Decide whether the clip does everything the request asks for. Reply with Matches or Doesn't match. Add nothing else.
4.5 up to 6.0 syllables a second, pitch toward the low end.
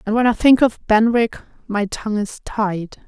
Doesn't match